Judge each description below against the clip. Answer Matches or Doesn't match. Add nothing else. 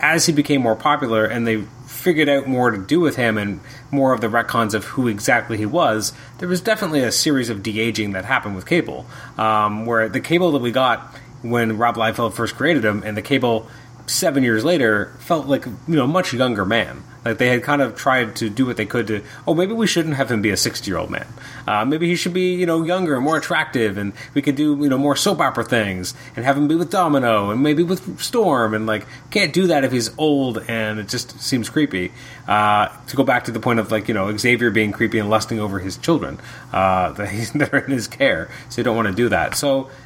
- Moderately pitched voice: Doesn't match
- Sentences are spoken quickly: Matches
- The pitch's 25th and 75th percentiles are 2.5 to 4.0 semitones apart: Doesn't match